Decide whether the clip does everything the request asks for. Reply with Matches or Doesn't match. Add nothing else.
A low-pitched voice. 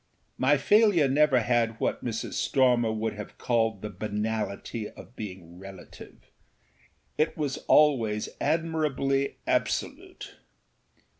Matches